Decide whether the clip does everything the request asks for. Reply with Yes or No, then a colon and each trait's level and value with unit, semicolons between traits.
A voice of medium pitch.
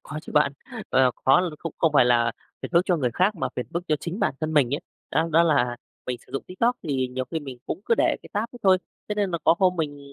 Yes: medium, 155 Hz